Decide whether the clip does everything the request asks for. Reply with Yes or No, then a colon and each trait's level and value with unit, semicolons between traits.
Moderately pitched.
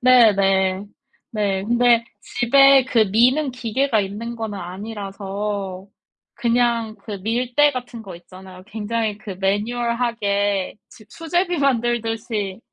No: high, 225 Hz